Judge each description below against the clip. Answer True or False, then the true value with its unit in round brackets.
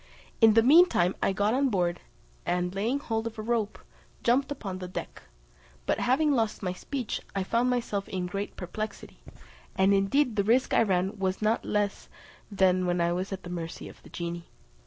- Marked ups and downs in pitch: False (4.0 semitones)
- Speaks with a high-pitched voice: True (200 Hz)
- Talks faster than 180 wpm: True (190 wpm)